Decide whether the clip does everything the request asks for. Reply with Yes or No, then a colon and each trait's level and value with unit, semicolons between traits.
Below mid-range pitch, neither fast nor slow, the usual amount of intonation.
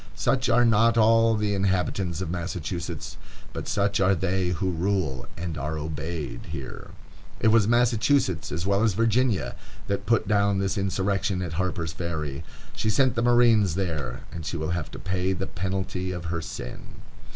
Yes: very low, 95 Hz; average, 170 wpm; average, 3.8 semitones